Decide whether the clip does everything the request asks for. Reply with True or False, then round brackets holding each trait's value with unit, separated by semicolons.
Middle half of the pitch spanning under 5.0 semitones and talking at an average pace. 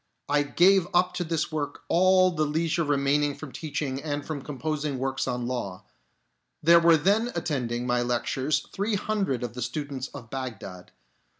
True (4.5 semitones; 165 wpm)